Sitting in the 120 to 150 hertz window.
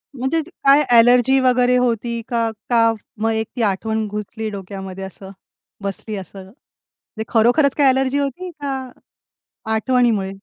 No: high, 235 Hz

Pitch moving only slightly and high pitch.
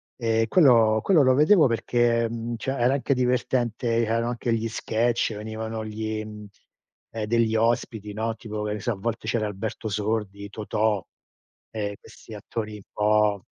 No: narrow, 1.7 semitones; low, 110 Hz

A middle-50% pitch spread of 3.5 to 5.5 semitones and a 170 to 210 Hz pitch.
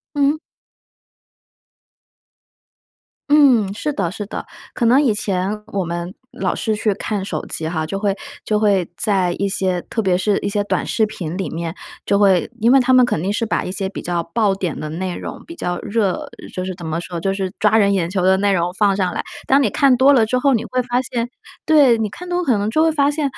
Yes: average, 4.5 semitones; high, 205 Hz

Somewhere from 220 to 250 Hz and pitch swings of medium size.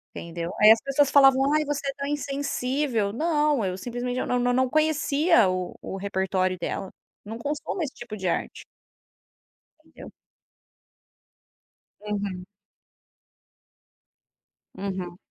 No: high, 245 Hz; wide, 6.7 semitones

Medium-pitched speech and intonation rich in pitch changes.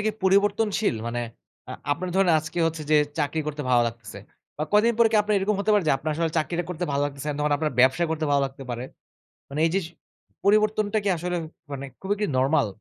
Yes: medium, 160 Hz; wide, 6.1 semitones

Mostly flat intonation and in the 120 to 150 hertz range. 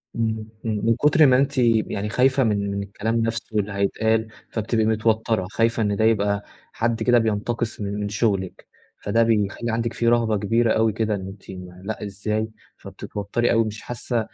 No: narrow, 2.0 semitones; low, 110 Hz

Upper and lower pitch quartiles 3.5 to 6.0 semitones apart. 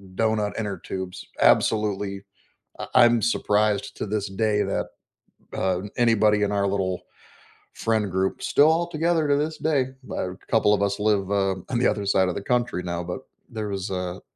No: average, 2.8 semitones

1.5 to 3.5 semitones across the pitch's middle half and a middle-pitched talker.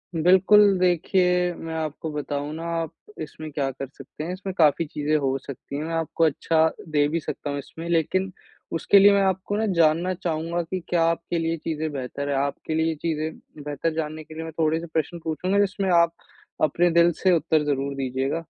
Yes: narrow, 2.5 semitones; medium, 160 Hz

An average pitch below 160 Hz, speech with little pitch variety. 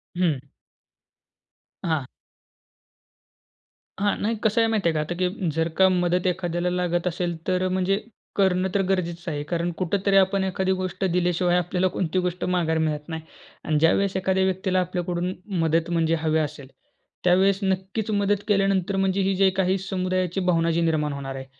No: medium, 180 Hz; narrow, 2.2 semitones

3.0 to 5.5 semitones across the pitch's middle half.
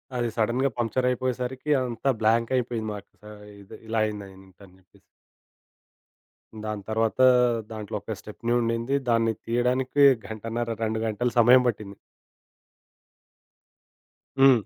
No: narrow, 2.4 semitones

